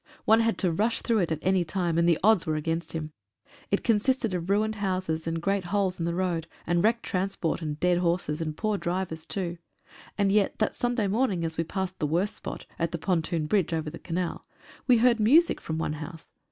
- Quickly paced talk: Yes, fast, 220 wpm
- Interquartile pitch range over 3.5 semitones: Yes, average, 3.9 semitones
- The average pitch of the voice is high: No, medium, 180 Hz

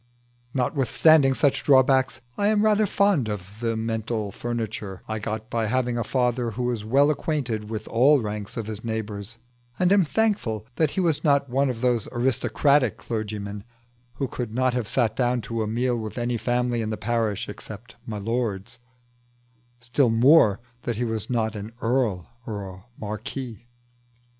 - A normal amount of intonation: Yes, average, 3.3 semitones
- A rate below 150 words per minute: No, average, 165 wpm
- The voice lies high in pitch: No, low, 120 Hz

